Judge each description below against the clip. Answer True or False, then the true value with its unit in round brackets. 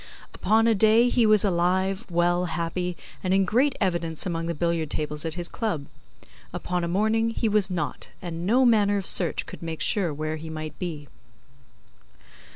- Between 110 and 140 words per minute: False (175 wpm)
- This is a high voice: False (180 Hz)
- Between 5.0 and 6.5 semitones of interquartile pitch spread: False (4.2 semitones)